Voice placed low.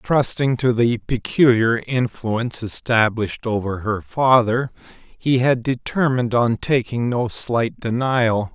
Yes: low, 120 Hz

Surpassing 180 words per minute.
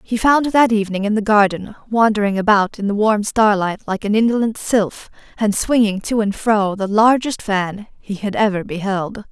Yes: average, 195 wpm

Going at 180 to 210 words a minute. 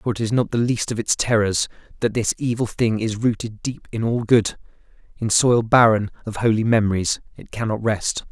Yes: average, 200 wpm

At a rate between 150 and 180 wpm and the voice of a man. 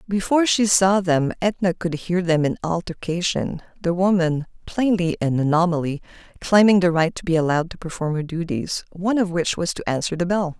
No: average, 175 wpm; female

